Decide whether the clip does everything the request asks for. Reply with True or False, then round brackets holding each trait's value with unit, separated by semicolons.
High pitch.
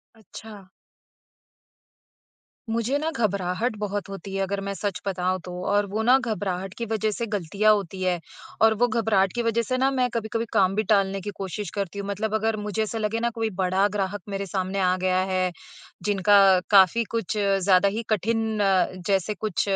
True (205 Hz)